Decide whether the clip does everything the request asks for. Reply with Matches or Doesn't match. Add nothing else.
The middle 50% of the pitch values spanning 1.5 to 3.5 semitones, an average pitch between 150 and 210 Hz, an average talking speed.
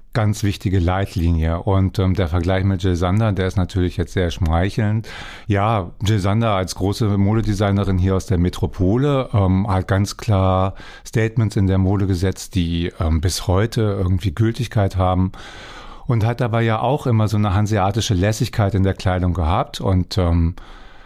Doesn't match